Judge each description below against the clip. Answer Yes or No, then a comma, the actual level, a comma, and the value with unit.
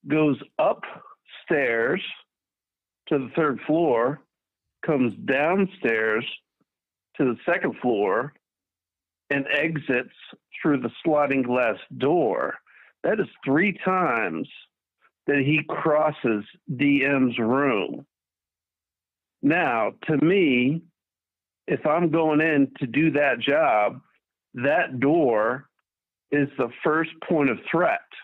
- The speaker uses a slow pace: Yes, slow, 100 wpm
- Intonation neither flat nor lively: No, wide, 6.6 semitones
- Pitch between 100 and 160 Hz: Yes, medium, 140 Hz